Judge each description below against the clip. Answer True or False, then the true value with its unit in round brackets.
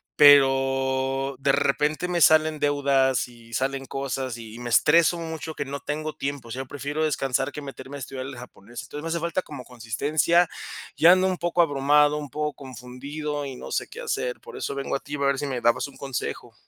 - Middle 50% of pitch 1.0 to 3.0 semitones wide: True (2.6 semitones)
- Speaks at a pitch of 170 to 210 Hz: False (140 Hz)